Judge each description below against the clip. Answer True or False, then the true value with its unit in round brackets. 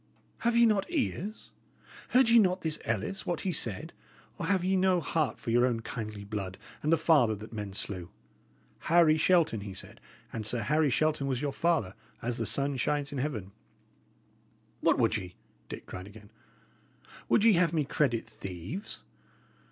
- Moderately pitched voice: True (145 Hz)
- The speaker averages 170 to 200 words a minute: True (175 wpm)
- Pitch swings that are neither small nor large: False (8.1 semitones)